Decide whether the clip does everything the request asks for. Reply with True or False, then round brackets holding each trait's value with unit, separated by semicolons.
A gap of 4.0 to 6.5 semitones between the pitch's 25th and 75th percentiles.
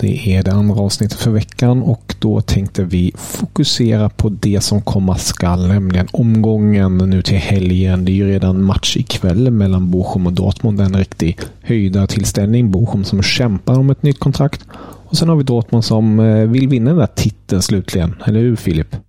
False (3.4 semitones)